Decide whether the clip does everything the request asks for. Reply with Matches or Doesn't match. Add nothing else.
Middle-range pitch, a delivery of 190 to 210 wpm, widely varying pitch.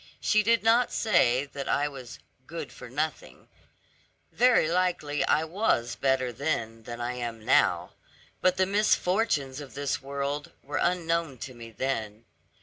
Doesn't match